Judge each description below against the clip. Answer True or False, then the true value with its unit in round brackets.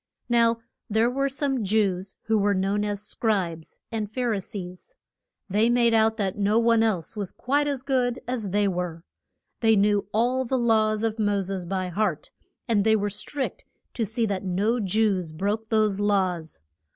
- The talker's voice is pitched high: True (215 Hz)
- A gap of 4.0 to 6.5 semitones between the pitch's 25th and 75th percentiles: False (2.9 semitones)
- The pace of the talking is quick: False (175 wpm)